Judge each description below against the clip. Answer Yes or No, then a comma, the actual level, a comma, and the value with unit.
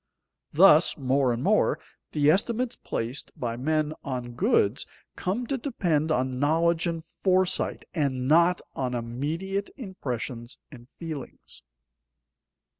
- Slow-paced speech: Yes, slow, 115 wpm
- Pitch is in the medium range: Yes, medium, 150 Hz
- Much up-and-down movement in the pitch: Yes, wide, 5.9 semitones